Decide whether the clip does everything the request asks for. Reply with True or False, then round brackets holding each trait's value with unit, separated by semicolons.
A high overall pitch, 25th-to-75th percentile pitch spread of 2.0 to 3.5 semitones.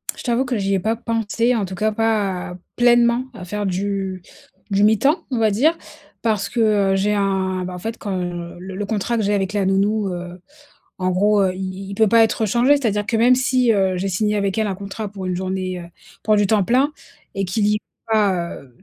True (205 Hz; 3.0 semitones)